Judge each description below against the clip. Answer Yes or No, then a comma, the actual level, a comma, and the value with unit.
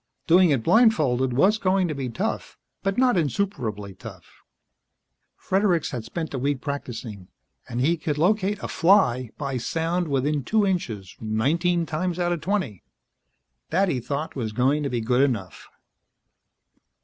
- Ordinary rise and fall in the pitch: No, wide, 6.6 semitones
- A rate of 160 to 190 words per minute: No, average, 150 wpm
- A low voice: No, medium, 150 Hz